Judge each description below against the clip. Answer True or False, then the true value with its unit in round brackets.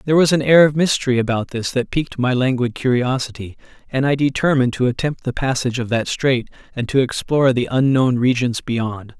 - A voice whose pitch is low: True (130 Hz)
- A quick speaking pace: False (195 wpm)